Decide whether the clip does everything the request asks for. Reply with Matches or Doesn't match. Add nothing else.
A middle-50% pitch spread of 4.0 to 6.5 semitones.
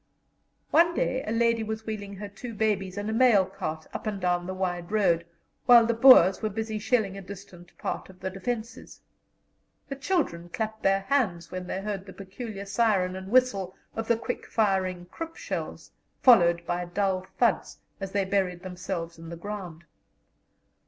Doesn't match